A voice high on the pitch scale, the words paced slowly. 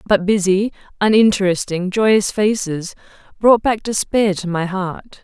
Yes: high, 200 Hz; slow, 125 wpm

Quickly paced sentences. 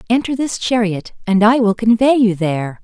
No: average, 190 wpm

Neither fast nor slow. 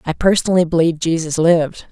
Yes: average, 155 wpm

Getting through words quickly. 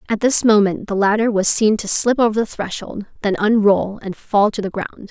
Yes: fast, 225 wpm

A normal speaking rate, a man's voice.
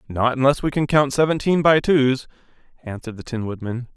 Yes: average, 180 wpm; male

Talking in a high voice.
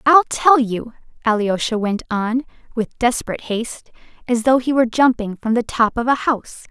Yes: high, 240 Hz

